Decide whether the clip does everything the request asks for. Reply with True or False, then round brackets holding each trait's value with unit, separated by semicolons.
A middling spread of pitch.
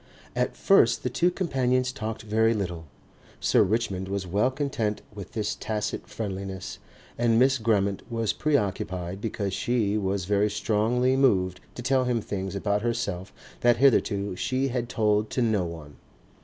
True (3.9 semitones)